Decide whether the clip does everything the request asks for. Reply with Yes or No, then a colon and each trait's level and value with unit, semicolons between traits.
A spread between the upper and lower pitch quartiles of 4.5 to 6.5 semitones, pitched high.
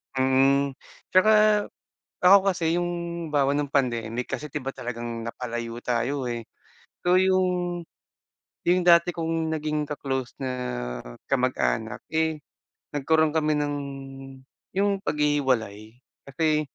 No: average, 5.0 semitones; medium, 150 Hz